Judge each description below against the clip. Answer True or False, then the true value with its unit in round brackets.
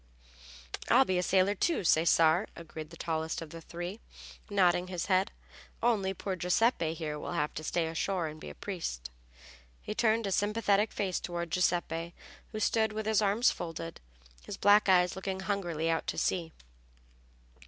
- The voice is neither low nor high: True (180 Hz)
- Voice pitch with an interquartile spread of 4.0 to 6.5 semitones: False (3.6 semitones)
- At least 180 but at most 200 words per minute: False (165 wpm)